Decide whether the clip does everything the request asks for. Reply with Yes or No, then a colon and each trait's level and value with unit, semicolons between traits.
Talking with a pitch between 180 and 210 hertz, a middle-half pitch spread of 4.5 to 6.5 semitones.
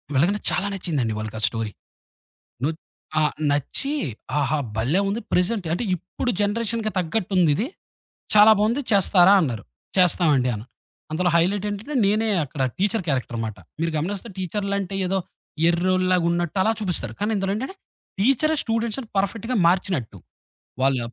Yes: medium, 185 Hz; average, 5.2 semitones